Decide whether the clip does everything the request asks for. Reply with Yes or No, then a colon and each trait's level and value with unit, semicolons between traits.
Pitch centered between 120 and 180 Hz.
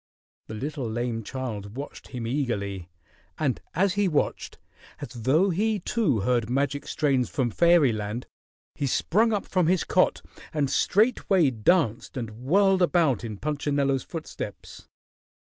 Yes: medium, 140 Hz